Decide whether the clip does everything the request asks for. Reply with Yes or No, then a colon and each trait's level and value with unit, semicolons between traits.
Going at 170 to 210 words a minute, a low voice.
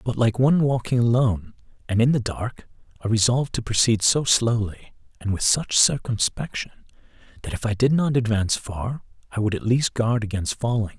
Yes: average, 180 wpm; low, 115 Hz